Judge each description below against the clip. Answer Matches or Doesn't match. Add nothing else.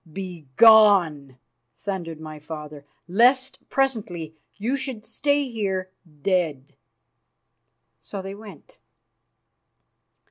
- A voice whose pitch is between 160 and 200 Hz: Matches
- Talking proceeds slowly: Matches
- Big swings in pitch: Matches